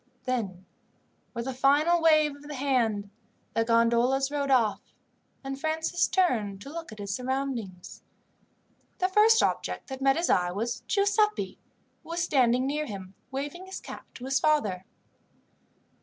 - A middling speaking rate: Yes, average, 150 wpm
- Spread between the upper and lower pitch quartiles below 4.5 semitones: No, average, 5.0 semitones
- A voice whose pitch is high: Yes, very high, 270 Hz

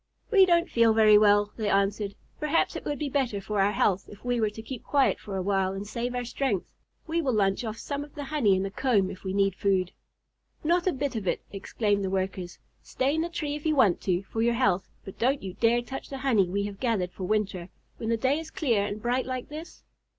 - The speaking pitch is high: Yes, high, 220 Hz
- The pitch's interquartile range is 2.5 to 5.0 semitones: No, wide, 5.4 semitones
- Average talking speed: No, fast, 245 wpm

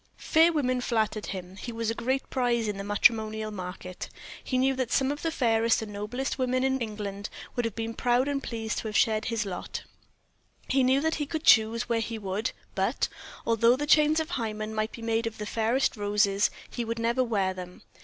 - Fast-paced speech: Yes, fast, 210 wpm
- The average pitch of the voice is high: Yes, high, 230 Hz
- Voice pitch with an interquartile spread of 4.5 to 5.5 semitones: No, average, 3.2 semitones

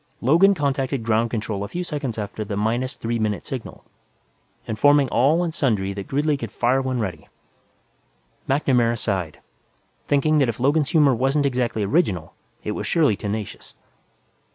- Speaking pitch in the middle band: No, low, 125 Hz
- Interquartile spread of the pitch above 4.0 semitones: Yes, average, 4.9 semitones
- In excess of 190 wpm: No, average, 155 wpm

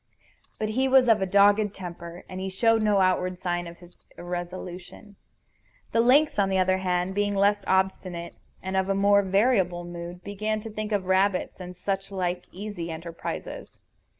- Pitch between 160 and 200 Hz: Yes, high, 190 Hz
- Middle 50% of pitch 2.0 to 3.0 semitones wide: Yes, narrow, 2.4 semitones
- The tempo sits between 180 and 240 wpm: No, average, 165 wpm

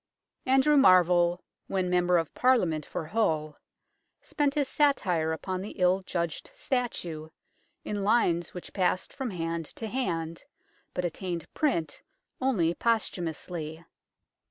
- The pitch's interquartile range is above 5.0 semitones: Yes, wide, 5.5 semitones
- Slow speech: Yes, slow, 120 wpm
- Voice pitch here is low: No, medium, 180 Hz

